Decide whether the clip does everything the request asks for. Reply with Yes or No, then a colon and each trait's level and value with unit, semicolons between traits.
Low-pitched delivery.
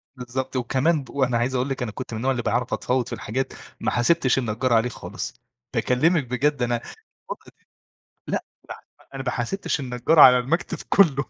Yes: low, 130 Hz